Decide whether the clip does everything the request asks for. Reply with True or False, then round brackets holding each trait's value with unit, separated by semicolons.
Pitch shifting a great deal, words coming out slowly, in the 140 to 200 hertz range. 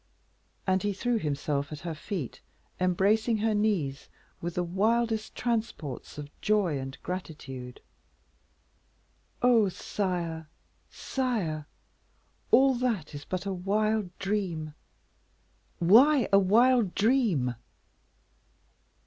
True (5.7 semitones; 100 wpm; 190 Hz)